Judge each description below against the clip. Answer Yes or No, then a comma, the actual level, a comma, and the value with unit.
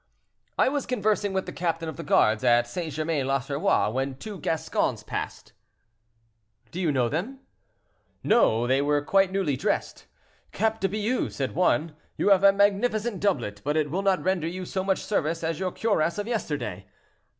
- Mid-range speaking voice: Yes, medium, 175 Hz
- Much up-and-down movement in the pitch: Yes, wide, 5.8 semitones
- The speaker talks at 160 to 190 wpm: Yes, average, 175 wpm